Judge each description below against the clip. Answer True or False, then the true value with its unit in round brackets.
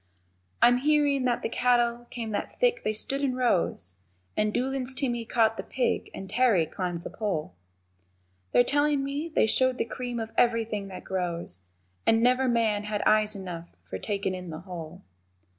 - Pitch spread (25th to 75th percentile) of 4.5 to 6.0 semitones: True (4.9 semitones)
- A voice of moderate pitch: False (230 Hz)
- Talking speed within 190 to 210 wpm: False (175 wpm)